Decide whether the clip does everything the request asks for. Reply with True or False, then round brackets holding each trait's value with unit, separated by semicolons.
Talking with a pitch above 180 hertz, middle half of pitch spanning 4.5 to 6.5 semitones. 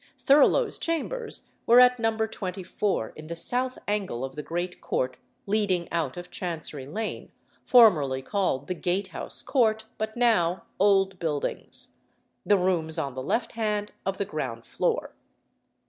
True (190 Hz; 5.6 semitones)